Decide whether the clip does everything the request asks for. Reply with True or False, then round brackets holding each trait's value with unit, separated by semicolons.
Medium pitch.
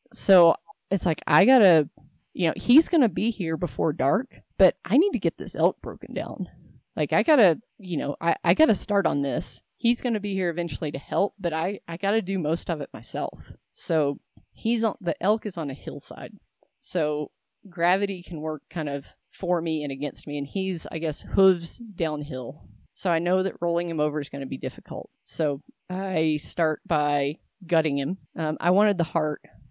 True (170 Hz)